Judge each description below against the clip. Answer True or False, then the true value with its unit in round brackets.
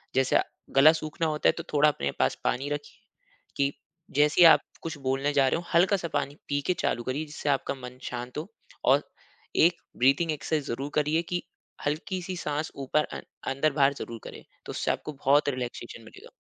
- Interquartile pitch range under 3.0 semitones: True (2.5 semitones)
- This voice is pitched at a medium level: True (145 Hz)